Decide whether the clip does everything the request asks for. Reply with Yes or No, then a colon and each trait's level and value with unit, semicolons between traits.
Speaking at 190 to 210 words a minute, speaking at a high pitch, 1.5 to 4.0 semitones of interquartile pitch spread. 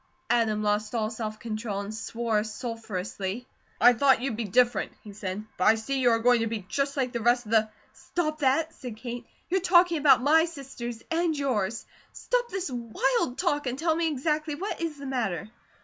No: average, 200 wpm; high, 245 Hz; average, 5.0 semitones